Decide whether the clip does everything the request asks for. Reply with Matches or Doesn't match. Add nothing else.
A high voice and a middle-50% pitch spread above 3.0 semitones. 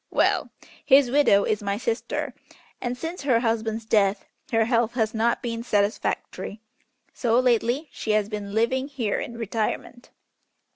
Doesn't match